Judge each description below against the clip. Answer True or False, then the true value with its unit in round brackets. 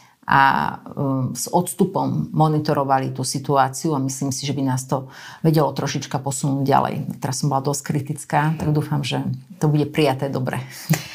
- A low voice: False (145 Hz)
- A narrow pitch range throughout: True (2.2 semitones)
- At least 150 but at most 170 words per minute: True (155 wpm)